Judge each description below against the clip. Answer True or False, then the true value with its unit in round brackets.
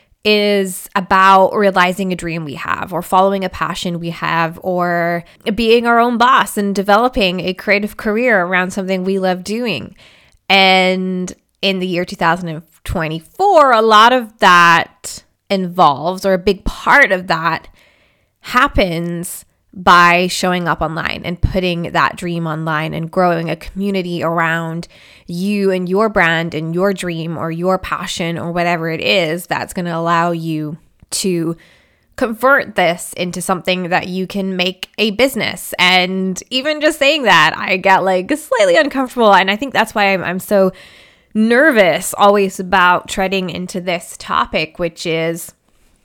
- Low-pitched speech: False (185 Hz)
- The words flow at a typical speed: True (150 wpm)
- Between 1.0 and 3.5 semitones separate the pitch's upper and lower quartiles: True (2.9 semitones)